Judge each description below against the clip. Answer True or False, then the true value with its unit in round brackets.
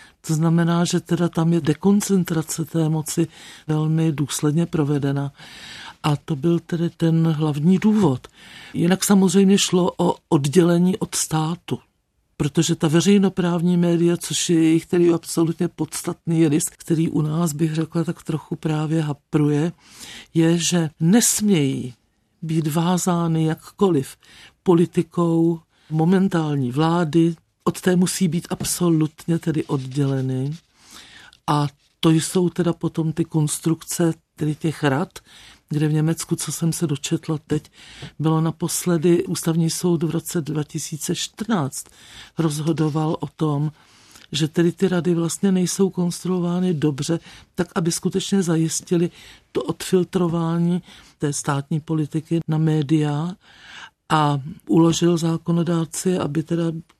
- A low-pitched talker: False (165 Hz)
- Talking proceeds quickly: False (120 wpm)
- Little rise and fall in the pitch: True (2.0 semitones)